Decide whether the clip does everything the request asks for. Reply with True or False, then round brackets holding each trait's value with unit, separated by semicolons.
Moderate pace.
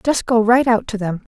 False (265 wpm)